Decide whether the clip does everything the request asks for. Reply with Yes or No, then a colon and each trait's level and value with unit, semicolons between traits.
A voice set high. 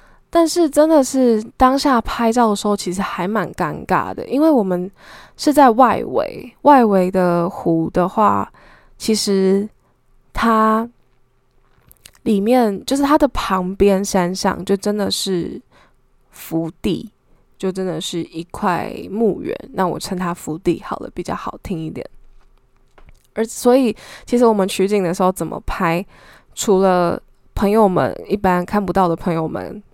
Yes: high, 195 Hz